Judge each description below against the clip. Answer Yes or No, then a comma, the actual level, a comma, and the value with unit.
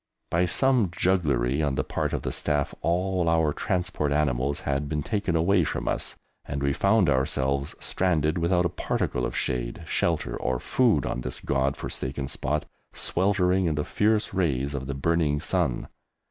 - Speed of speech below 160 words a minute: No, average, 170 wpm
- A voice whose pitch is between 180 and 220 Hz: No, very low, 75 Hz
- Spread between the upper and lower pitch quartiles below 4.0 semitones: No, average, 4.7 semitones